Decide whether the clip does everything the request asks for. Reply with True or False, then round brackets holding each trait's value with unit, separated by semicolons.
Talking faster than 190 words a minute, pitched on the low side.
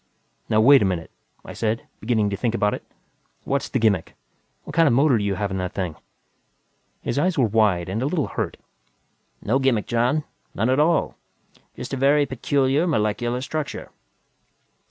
False (175 wpm; 120 Hz)